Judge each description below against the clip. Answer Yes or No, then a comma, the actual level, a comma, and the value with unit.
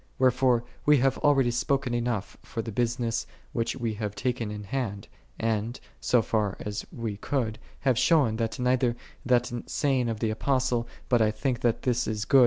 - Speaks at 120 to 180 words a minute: No, average, 195 wpm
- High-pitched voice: No, low, 120 Hz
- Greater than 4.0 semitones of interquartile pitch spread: No, narrow, 2.6 semitones